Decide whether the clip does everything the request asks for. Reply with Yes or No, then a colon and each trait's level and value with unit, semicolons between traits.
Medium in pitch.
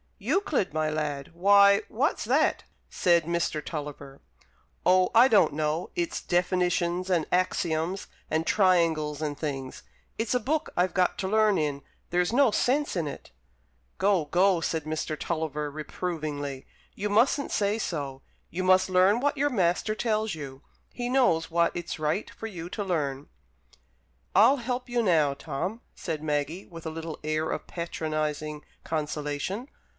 Yes: medium, 170 Hz